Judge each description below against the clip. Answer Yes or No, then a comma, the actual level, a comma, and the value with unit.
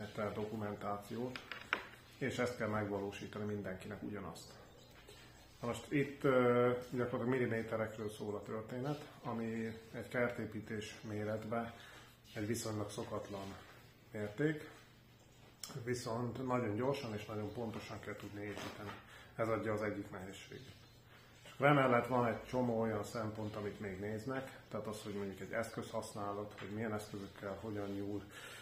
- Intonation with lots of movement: No, average, 2.8 semitones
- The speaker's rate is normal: Yes, average, 125 wpm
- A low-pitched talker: Yes, low, 110 Hz